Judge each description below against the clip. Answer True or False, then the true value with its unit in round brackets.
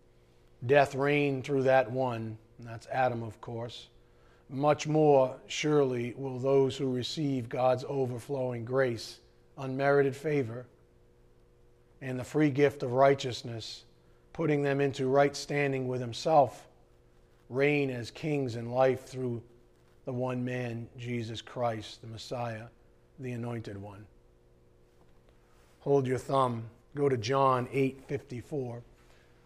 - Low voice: True (125 Hz)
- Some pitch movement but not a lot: False (6.6 semitones)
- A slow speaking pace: True (120 wpm)